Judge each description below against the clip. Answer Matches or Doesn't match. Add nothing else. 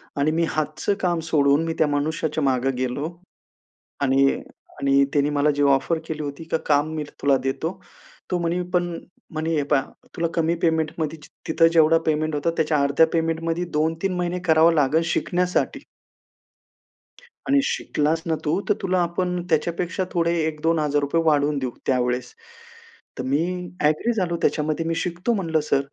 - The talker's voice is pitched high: Doesn't match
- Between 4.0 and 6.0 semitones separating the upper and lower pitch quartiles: Doesn't match